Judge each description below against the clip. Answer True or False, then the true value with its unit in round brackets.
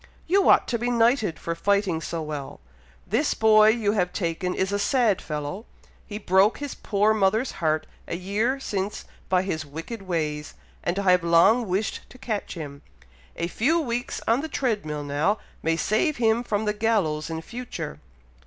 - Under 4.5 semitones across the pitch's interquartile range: False (5.3 semitones)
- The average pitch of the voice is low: False (200 Hz)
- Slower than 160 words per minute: False (180 wpm)